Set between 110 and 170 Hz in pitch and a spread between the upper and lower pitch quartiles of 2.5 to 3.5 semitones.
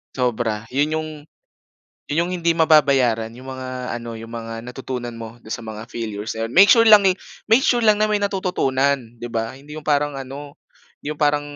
No: low, 135 Hz; average, 5.3 semitones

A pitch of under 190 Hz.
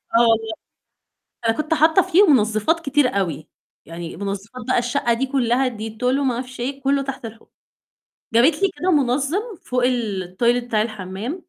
No: high, 245 Hz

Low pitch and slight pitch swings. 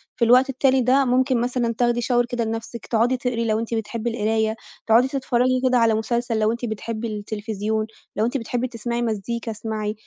No: high, 235 Hz; narrow, 2.0 semitones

